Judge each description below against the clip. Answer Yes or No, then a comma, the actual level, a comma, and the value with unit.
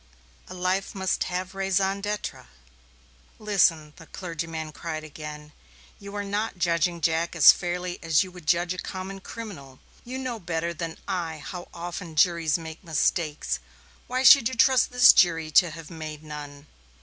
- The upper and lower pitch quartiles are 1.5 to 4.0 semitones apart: Yes, average, 3.4 semitones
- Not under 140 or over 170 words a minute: Yes, average, 160 wpm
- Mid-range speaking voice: Yes, medium, 175 Hz